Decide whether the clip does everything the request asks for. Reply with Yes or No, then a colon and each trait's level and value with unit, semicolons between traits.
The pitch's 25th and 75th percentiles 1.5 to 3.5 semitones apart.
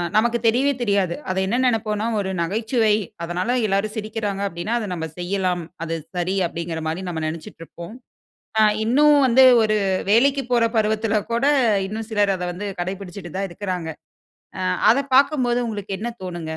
No: average, 4.2 semitones